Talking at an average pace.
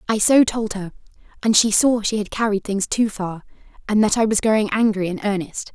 No: fast, 220 wpm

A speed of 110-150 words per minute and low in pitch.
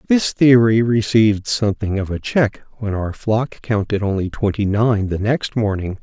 No: average, 170 wpm; low, 110 Hz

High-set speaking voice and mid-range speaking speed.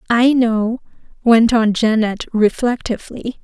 No: high, 230 Hz; slow, 105 wpm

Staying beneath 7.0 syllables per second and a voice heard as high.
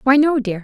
Yes: 5.7 syllables/s; very high, 255 Hz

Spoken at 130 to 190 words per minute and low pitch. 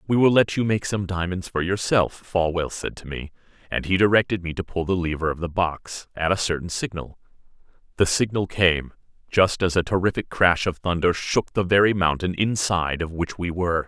No: fast, 205 wpm; very low, 90 Hz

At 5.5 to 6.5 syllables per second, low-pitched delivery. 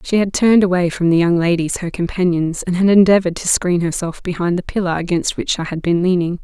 No: 6.0 syllables/s; medium, 175 Hz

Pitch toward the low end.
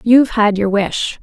No: high, 215 Hz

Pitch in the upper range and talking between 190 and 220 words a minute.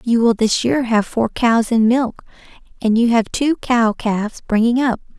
Yes: high, 230 Hz; average, 195 wpm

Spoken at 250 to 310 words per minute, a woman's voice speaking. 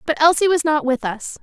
Yes: fast, 255 wpm; female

